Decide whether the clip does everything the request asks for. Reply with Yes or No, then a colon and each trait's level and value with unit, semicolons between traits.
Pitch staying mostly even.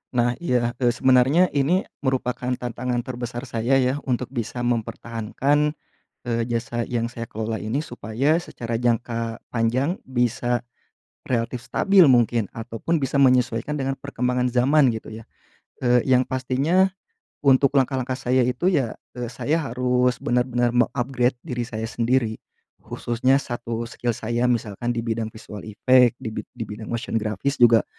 Yes: narrow, 2.0 semitones